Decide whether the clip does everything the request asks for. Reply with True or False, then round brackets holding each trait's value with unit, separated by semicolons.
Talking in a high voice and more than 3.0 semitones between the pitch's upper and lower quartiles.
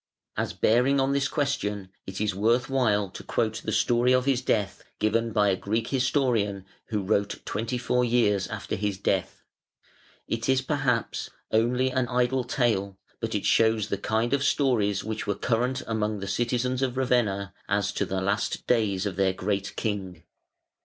False (110 Hz; 3.6 semitones)